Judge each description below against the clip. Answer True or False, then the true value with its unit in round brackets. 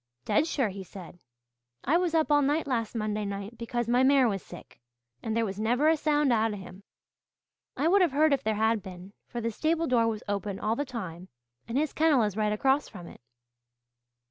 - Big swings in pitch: True (5.7 semitones)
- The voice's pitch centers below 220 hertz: False (230 Hz)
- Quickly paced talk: True (215 wpm)